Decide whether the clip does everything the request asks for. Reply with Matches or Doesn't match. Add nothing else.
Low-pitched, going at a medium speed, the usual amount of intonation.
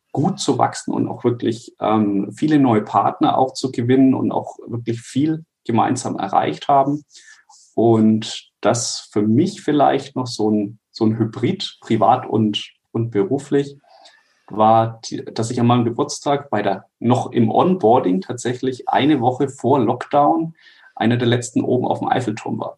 Matches